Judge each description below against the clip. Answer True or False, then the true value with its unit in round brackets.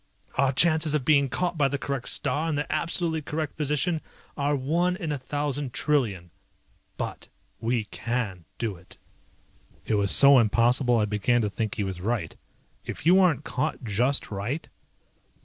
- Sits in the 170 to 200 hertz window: False (135 Hz)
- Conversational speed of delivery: True (165 wpm)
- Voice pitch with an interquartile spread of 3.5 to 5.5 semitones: True (5.2 semitones)